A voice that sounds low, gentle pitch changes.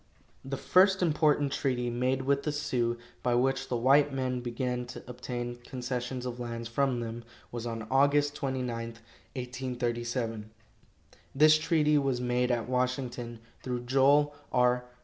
Yes: low, 125 Hz; narrow, 2.2 semitones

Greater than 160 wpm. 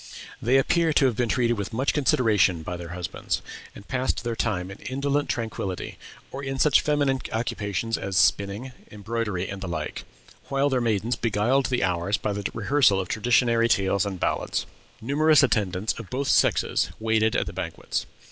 Yes: average, 175 wpm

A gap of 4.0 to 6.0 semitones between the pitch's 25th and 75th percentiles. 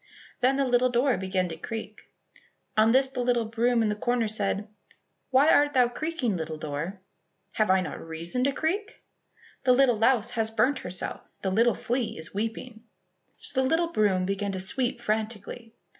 Yes: average, 4.3 semitones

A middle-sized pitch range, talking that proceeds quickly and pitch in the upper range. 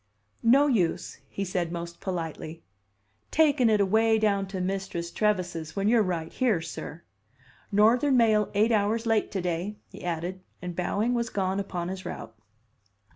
No: average, 4.0 semitones; average, 155 wpm; high, 195 Hz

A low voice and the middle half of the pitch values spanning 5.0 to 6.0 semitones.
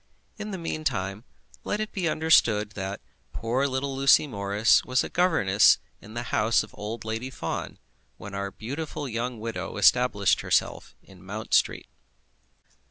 Yes: low, 115 Hz; average, 5.3 semitones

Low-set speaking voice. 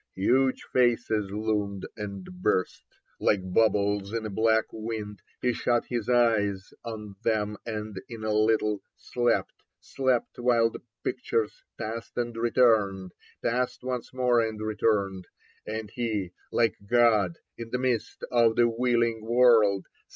Yes: low, 110 Hz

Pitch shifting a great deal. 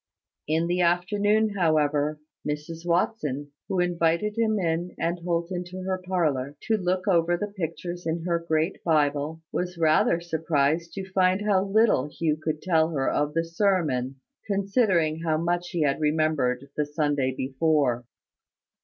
No: average, 3.3 semitones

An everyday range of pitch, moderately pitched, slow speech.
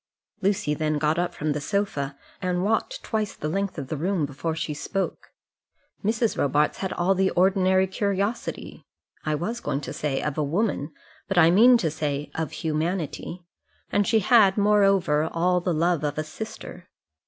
No: average, 4.6 semitones; medium, 175 Hz; average, 175 wpm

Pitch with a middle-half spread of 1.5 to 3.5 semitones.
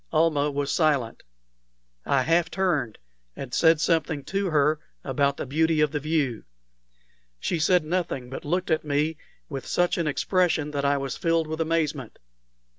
Yes: average, 2.8 semitones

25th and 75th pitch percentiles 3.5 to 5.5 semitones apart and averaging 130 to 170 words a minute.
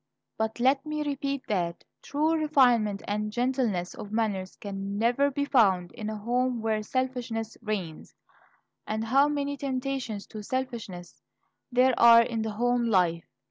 Yes: average, 3.9 semitones; average, 145 wpm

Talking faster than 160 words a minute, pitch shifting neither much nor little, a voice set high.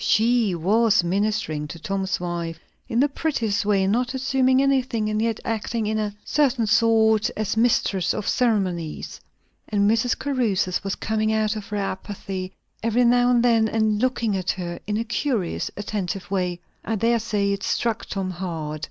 Yes: average, 170 wpm; average, 3.3 semitones; high, 215 Hz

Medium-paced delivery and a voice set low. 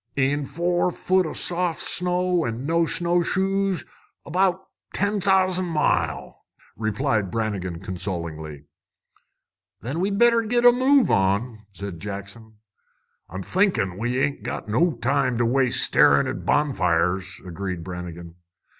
No: slow, 125 wpm; low, 130 Hz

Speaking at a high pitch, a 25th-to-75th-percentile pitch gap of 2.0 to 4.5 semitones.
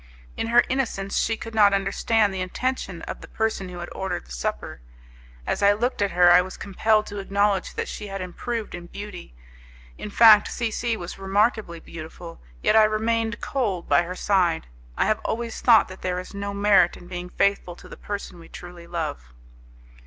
Yes: high, 200 Hz; average, 3.5 semitones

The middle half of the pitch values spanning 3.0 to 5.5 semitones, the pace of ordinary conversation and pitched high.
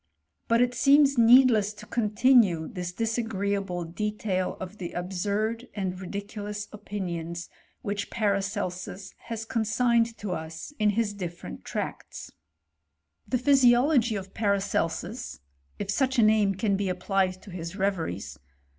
No: average, 3.6 semitones; slow, 130 wpm; high, 205 Hz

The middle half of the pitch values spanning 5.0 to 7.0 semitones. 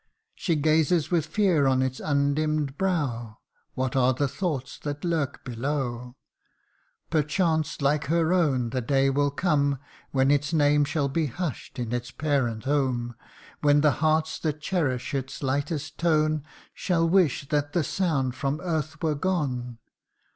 No: average, 3.0 semitones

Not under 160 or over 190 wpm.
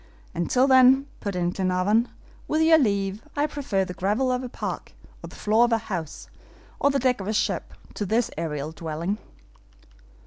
Yes: average, 185 wpm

